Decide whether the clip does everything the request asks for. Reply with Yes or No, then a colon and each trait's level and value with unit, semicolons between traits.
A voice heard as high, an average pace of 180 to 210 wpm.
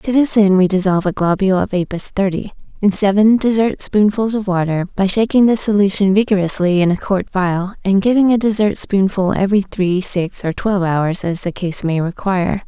Yes: high, 195 Hz; average, 195 wpm